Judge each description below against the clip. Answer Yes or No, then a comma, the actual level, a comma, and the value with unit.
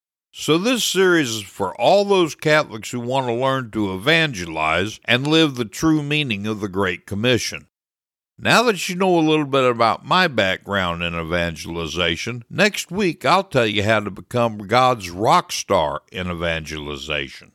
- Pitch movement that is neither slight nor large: No, wide, 9.0 semitones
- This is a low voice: Yes, low, 120 Hz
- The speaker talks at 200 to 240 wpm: No, average, 165 wpm